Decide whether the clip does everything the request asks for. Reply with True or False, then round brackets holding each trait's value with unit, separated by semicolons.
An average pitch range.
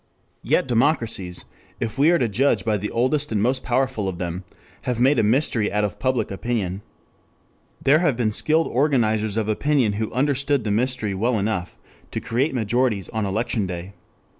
True (4.1 semitones)